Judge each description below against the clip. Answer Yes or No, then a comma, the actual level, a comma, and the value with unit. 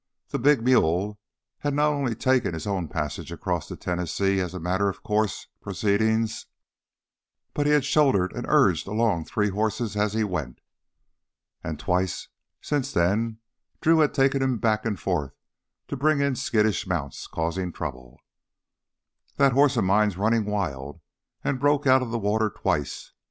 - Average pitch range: No, wide, 5.9 semitones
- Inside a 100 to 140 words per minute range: No, average, 155 wpm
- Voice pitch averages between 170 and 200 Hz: No, low, 105 Hz